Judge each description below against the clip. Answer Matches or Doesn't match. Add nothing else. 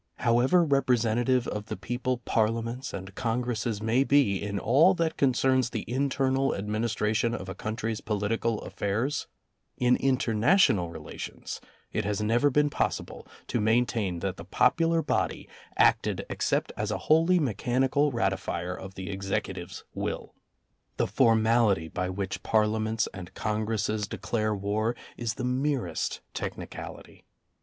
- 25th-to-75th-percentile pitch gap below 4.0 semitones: Matches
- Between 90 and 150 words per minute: Matches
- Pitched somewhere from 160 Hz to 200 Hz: Doesn't match